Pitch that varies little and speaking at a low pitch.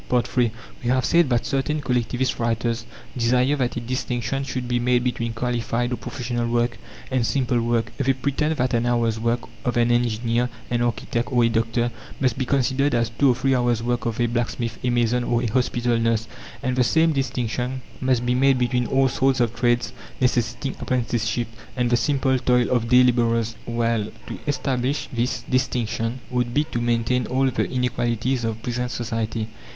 Yes: narrow, 1.5 semitones; low, 120 Hz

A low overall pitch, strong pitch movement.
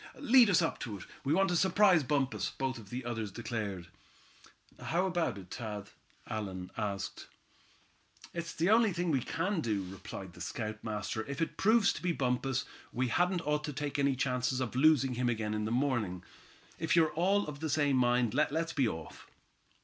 Yes: low, 130 Hz; wide, 7.0 semitones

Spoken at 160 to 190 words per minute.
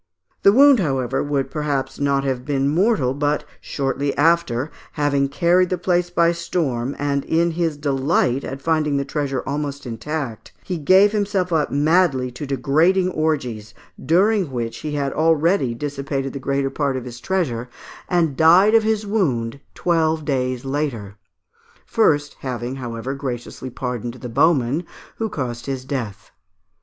No: average, 150 wpm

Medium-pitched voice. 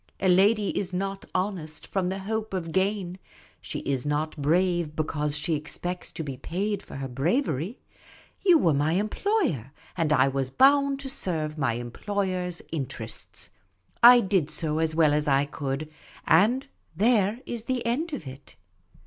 Yes: medium, 175 Hz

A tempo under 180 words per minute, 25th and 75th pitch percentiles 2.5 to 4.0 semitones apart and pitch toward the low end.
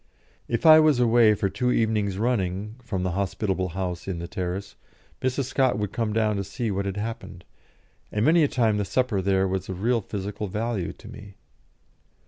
No: average, 190 wpm; average, 3.5 semitones; low, 105 Hz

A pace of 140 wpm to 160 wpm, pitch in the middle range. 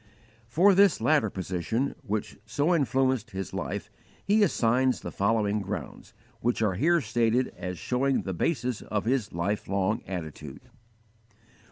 No: average, 145 wpm; low, 115 Hz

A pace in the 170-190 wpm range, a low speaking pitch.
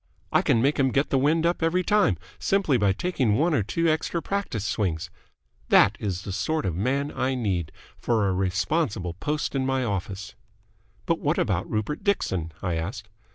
Yes: average, 185 wpm; low, 125 Hz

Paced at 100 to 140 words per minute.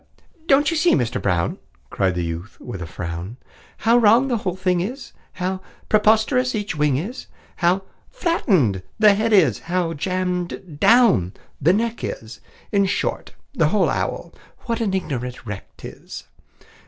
No: average, 155 wpm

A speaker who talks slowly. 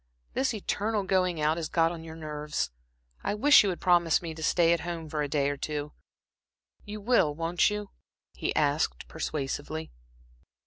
No: average, 175 wpm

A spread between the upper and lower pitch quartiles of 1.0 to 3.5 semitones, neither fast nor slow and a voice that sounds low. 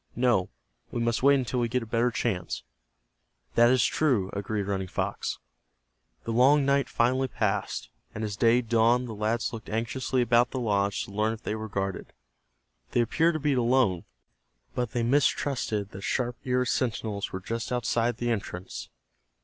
Yes: average, 2.9 semitones; average, 170 wpm; low, 115 Hz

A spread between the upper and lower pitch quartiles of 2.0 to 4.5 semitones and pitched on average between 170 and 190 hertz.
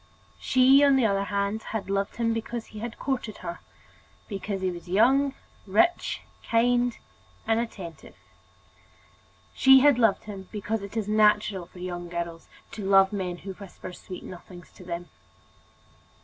No: average, 3.8 semitones; high, 205 Hz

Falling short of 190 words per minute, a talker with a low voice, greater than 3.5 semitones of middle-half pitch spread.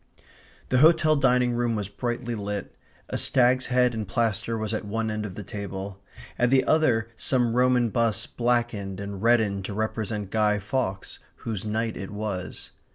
No: average, 165 wpm; low, 110 Hz; average, 3.0 semitones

